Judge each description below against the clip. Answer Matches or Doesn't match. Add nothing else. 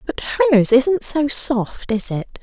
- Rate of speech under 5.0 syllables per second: Matches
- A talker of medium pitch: Doesn't match